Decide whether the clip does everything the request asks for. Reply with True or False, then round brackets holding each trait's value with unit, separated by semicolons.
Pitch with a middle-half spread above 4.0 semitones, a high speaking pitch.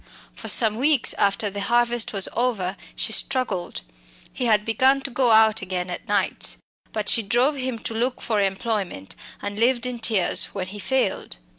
False (3.7 semitones; 220 Hz)